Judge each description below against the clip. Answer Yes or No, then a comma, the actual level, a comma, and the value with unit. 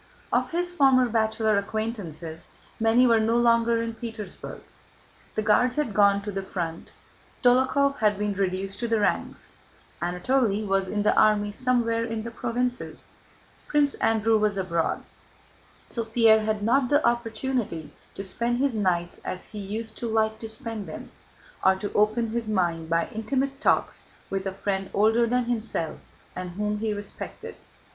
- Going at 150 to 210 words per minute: Yes, average, 160 wpm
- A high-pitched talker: Yes, high, 220 Hz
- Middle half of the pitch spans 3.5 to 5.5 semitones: No, average, 2.9 semitones